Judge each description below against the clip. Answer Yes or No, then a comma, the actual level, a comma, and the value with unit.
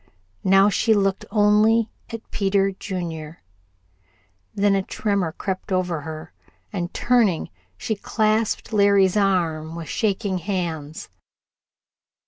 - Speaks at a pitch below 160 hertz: No, high, 195 Hz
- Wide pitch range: No, average, 3.3 semitones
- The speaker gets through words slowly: Yes, slow, 110 wpm